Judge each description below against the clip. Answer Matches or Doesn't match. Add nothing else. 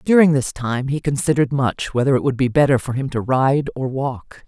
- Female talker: Matches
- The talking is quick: Matches